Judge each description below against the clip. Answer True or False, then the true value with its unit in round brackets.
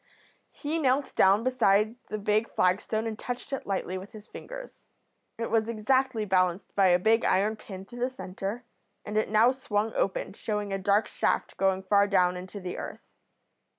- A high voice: True (210 Hz)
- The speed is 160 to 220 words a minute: True (180 wpm)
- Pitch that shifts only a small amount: False (3.1 semitones)